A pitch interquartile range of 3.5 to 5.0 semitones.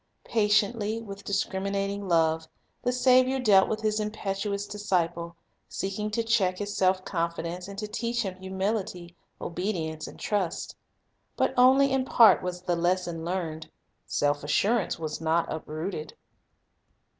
Yes: average, 3.8 semitones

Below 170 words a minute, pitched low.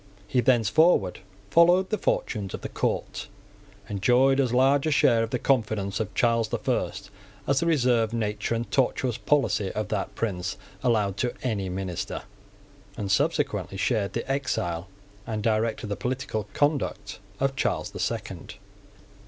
Yes: average, 150 wpm; low, 115 Hz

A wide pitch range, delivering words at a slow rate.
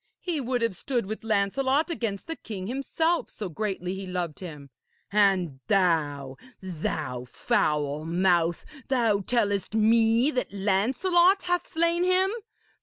Yes: wide, 6.8 semitones; slow, 130 wpm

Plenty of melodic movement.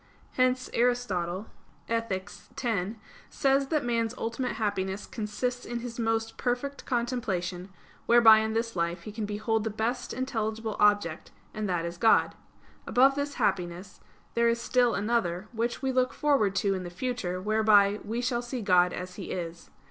No: average, 4.0 semitones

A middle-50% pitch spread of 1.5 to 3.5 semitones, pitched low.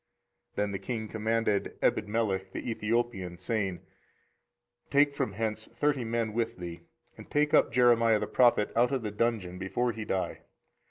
Yes: average, 3.0 semitones; low, 110 Hz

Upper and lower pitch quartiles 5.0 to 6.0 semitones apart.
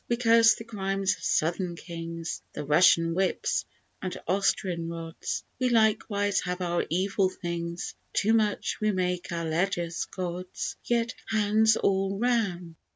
No: average, 3.7 semitones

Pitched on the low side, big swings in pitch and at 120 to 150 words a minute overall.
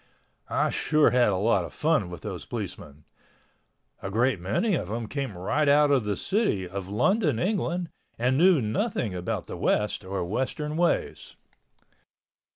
No: low, 120 Hz; wide, 7.8 semitones; average, 160 wpm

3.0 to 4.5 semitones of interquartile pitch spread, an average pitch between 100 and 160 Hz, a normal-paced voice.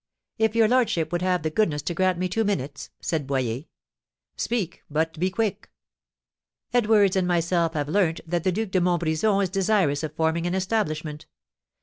No: average, 4.0 semitones; medium, 175 Hz; average, 170 wpm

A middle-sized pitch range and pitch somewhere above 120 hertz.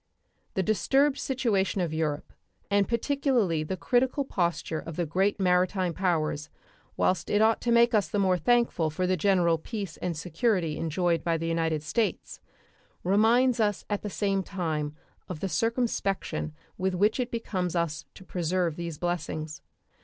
Yes: average, 4.7 semitones; medium, 185 Hz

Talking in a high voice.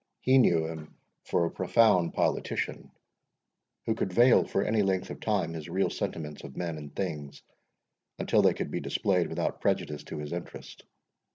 No: very low, 85 Hz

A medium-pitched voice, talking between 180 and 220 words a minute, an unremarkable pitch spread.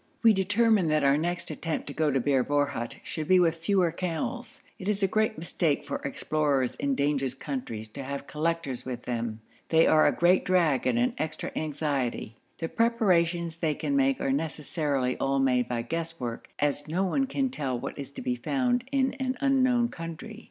No: medium, 160 Hz; average, 190 wpm; wide, 5.9 semitones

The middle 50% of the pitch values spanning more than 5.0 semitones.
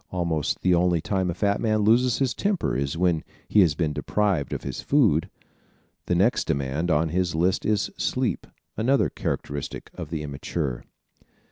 Yes: wide, 5.5 semitones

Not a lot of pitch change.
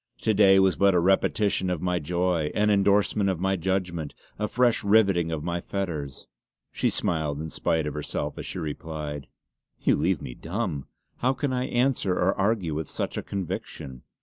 No: average, 4.0 semitones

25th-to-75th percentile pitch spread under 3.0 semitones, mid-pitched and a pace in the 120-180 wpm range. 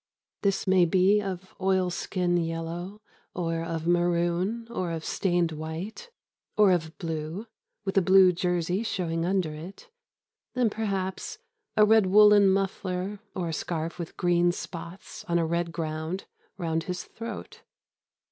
Yes: narrow, 2.6 semitones; medium, 180 Hz; average, 140 wpm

